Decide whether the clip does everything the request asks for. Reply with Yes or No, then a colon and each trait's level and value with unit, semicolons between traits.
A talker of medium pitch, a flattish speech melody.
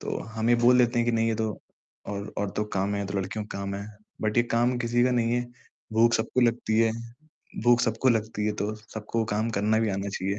No: low, 110 Hz; narrow, 2.3 semitones